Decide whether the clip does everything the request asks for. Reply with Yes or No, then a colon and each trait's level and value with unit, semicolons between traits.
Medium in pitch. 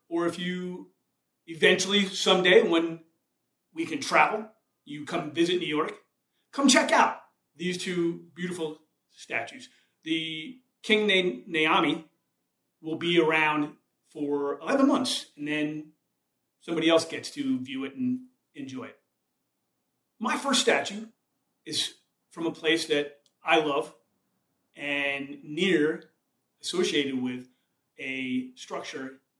Yes: medium, 170 Hz